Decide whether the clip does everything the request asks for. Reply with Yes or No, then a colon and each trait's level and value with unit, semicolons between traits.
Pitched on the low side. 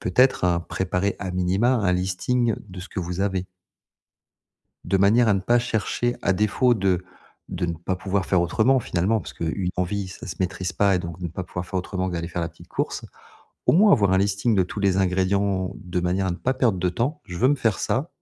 Yes: very low, 95 Hz